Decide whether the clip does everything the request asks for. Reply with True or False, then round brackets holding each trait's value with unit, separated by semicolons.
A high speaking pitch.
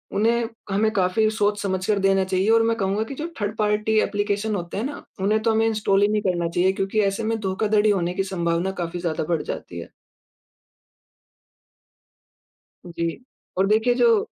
True (205 Hz)